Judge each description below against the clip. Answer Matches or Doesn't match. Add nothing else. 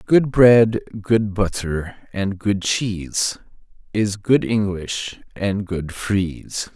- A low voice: Matches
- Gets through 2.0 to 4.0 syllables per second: Matches